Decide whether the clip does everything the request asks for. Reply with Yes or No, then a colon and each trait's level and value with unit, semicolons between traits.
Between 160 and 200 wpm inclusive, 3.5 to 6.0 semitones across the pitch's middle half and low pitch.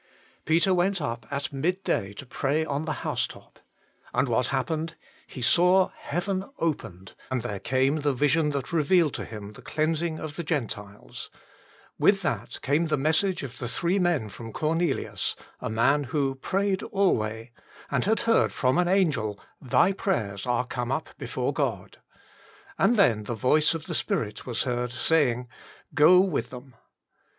No: average, 170 wpm; wide, 5.6 semitones; medium, 145 Hz